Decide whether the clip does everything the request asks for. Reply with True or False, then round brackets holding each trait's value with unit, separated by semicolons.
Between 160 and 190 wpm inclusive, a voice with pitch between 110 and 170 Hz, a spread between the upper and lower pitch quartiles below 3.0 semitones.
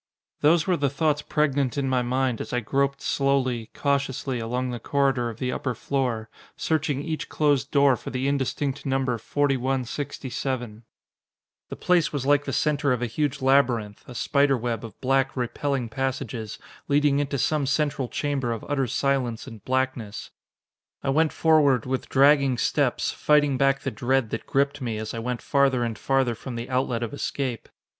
True (170 wpm; 135 Hz; 2.5 semitones)